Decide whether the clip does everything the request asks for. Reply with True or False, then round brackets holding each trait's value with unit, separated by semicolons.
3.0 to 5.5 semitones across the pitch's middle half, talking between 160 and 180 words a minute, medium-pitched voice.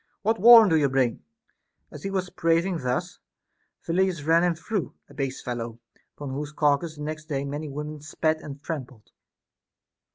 True (3.4 semitones; 170 wpm; 155 Hz)